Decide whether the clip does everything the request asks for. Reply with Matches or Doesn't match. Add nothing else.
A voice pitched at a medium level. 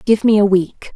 Doesn't match